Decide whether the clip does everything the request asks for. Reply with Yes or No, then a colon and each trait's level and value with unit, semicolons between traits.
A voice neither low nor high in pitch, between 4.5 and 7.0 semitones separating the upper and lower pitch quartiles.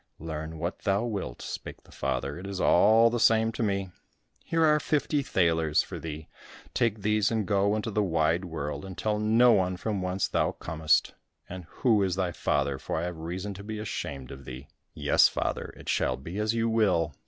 No: very low, 95 Hz; average, 4.9 semitones